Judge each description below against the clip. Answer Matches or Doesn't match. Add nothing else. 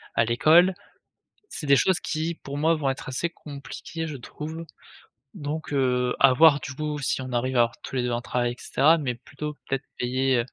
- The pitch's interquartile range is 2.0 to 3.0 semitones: Doesn't match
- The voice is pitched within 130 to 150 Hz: Matches